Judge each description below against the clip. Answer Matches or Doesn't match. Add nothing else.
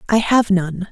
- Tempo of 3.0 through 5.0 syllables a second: Matches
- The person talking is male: Doesn't match